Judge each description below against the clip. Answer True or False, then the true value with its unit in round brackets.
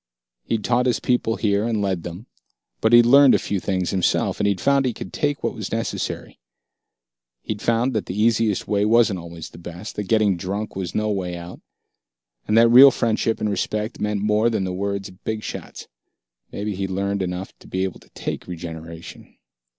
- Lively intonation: False (3.4 semitones)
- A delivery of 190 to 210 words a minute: True (195 wpm)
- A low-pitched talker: True (105 Hz)